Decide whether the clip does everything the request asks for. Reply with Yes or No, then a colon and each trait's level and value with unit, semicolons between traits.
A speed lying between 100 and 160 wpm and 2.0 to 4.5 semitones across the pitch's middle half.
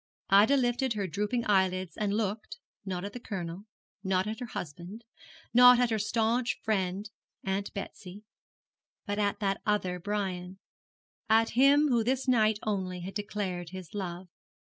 Yes: average, 150 wpm; average, 3.2 semitones